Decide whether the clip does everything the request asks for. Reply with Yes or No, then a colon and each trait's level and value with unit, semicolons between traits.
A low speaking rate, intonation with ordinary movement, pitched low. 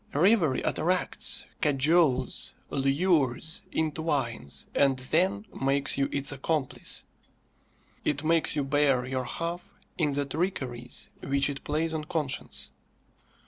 No: slow, 110 wpm; average, 3.2 semitones; medium, 145 Hz